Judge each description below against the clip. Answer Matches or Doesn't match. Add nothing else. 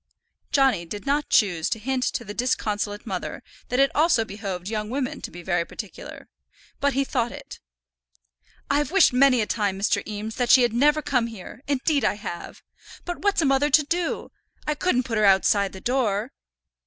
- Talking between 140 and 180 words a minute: Doesn't match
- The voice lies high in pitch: Matches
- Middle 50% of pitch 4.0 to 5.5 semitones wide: Matches